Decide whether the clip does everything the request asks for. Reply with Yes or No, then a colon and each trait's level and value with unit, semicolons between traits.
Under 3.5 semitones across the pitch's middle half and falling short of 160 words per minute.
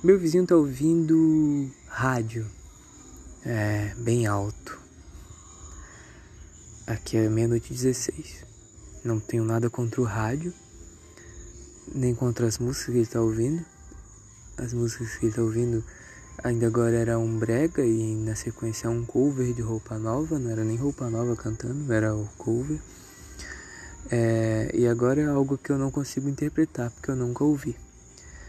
Yes: average, 3.0 semitones; average, 145 wpm